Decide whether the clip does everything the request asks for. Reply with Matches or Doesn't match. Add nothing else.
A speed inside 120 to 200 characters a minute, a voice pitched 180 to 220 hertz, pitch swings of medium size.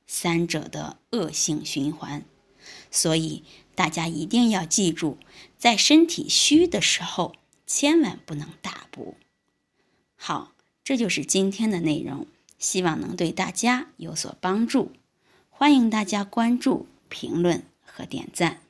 Doesn't match